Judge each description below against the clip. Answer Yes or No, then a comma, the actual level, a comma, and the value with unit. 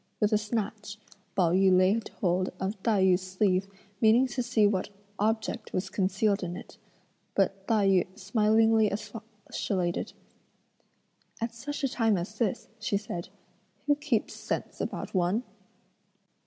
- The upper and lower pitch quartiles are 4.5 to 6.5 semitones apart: No, average, 2.9 semitones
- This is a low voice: No, high, 210 Hz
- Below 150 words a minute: Yes, average, 140 wpm